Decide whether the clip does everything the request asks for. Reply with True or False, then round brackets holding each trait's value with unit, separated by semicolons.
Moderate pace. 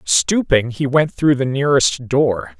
True (160 wpm)